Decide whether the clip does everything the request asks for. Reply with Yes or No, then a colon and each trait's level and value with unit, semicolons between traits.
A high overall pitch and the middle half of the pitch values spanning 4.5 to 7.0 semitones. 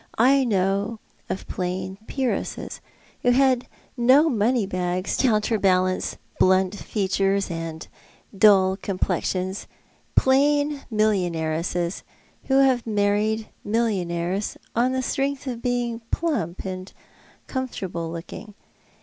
Yes: high, 205 Hz; average, 4.9 semitones